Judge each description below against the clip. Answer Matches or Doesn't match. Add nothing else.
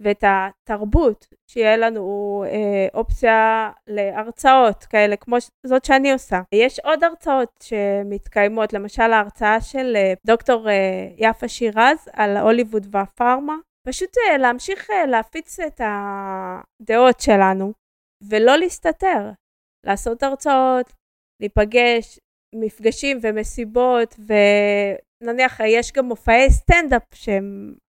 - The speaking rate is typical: Doesn't match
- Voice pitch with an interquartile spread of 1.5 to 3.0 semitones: Doesn't match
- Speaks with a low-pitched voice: Doesn't match